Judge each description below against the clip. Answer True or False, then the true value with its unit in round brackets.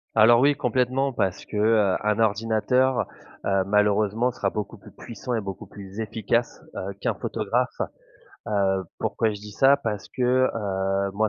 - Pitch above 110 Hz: False (105 Hz)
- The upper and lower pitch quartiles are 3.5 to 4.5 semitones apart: False (2.9 semitones)